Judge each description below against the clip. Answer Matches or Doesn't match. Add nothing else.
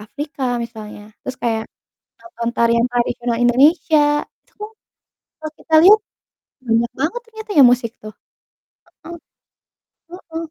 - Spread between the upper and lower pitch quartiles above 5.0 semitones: Matches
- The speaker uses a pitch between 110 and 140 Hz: Doesn't match